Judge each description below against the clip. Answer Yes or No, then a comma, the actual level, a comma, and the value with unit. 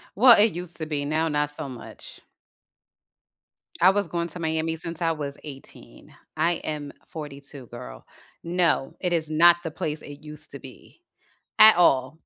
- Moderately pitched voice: Yes, medium, 155 Hz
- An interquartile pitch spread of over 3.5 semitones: No, average, 2.9 semitones